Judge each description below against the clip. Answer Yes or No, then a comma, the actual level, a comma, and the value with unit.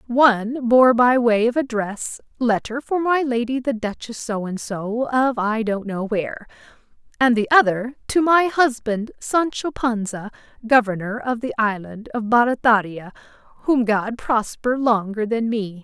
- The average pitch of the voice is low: No, high, 235 Hz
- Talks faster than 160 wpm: No, average, 150 wpm